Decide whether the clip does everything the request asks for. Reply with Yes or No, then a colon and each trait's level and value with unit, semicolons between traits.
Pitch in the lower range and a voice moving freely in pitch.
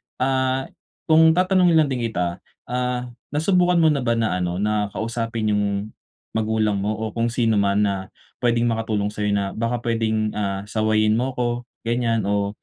No: low, 115 Hz; average, 3.1 semitones